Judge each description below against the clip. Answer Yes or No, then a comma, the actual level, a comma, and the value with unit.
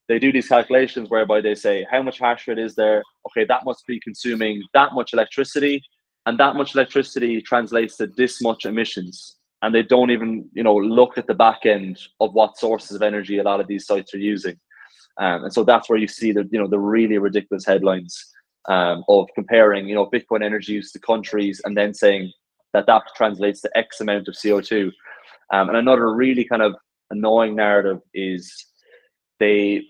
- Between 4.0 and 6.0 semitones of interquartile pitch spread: No, average, 2.9 semitones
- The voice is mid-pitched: No, low, 110 Hz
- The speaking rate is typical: Yes, average, 195 wpm